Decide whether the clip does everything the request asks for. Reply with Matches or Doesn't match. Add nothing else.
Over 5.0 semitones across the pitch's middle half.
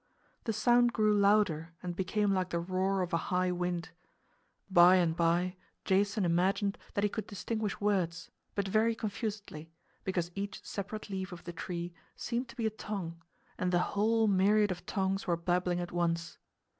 Doesn't match